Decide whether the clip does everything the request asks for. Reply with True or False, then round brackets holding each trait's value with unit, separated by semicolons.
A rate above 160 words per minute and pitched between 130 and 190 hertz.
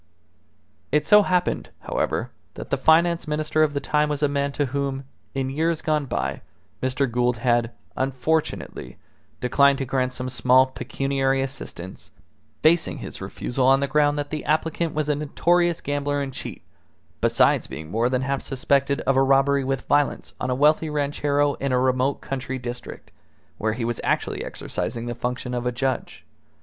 True (170 wpm; 135 Hz)